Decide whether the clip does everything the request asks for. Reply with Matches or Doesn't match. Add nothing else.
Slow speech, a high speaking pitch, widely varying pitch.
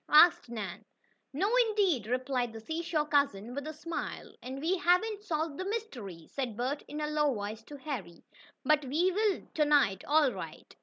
Doesn't match